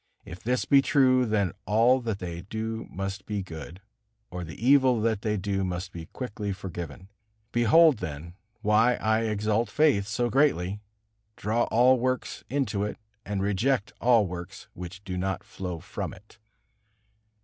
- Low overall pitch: Yes, low, 105 Hz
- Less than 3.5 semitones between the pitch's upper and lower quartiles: No, average, 4.1 semitones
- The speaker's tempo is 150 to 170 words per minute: Yes, average, 155 wpm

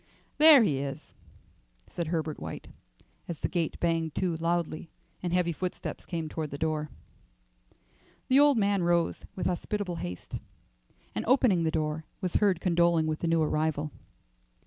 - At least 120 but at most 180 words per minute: Yes, average, 150 wpm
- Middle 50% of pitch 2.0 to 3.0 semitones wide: Yes, narrow, 2.6 semitones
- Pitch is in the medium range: Yes, medium, 170 Hz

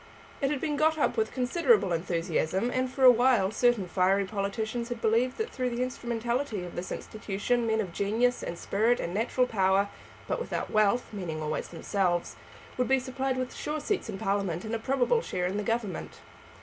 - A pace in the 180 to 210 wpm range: Yes, average, 190 wpm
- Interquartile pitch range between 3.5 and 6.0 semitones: Yes, average, 4.7 semitones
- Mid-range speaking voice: No, high, 225 Hz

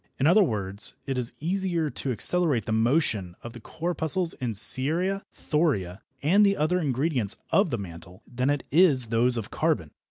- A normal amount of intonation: No, wide, 6.9 semitones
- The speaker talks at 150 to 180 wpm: Yes, average, 170 wpm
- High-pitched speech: No, low, 135 Hz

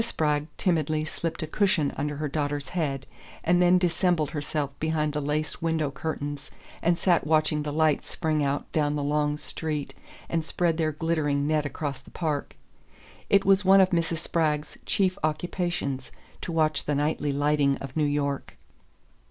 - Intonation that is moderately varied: No, narrow, 2.2 semitones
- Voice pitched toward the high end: No, medium, 155 Hz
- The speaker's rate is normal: Yes, average, 165 wpm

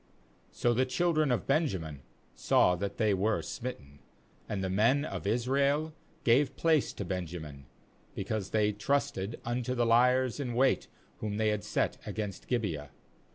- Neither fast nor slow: Yes, average, 155 wpm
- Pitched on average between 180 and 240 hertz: No, low, 115 Hz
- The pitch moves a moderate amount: Yes, average, 5.0 semitones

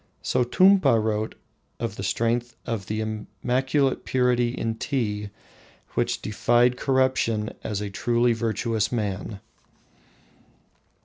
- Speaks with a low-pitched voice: Yes, low, 115 Hz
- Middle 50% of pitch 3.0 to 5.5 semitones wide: No, narrow, 2.6 semitones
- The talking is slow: Yes, slow, 105 wpm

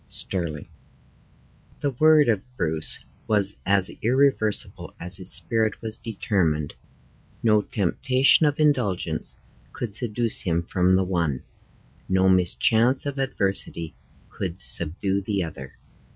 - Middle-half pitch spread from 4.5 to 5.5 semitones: Yes, average, 4.9 semitones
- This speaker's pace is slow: Yes, slow, 115 wpm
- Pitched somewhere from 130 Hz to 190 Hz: No, low, 100 Hz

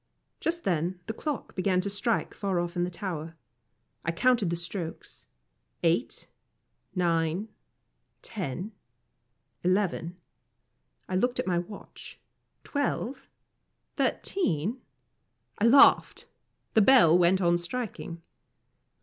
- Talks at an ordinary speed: No, slow, 105 wpm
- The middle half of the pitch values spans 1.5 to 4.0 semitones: No, average, 4.4 semitones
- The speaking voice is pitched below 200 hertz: Yes, medium, 185 Hz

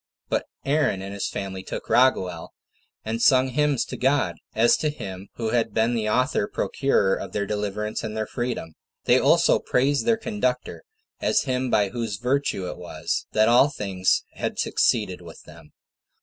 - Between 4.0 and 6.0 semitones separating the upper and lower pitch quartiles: Yes, average, 4.7 semitones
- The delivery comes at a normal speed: Yes, average, 170 wpm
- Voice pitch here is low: Yes, low, 115 Hz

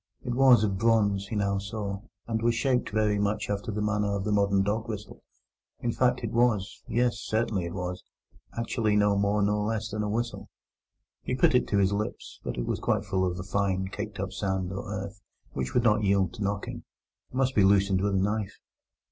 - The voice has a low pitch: Yes, low, 105 Hz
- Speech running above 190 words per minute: Yes, fast, 205 wpm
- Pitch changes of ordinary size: No, narrow, 2.1 semitones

